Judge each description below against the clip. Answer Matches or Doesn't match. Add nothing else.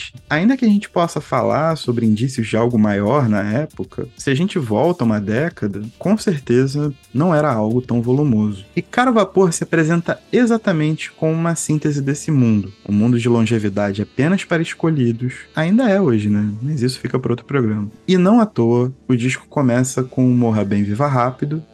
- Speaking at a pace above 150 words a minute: Matches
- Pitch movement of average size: Doesn't match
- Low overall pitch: Matches